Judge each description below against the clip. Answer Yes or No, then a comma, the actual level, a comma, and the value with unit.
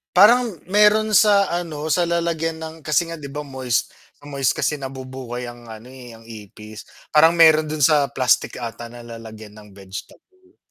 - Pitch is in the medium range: Yes, medium, 145 Hz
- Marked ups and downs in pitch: Yes, wide, 5.9 semitones